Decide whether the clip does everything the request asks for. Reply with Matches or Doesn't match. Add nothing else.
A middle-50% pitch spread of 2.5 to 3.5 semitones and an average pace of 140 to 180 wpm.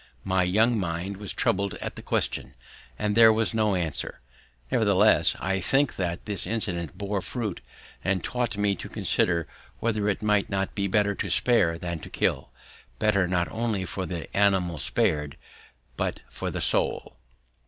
Matches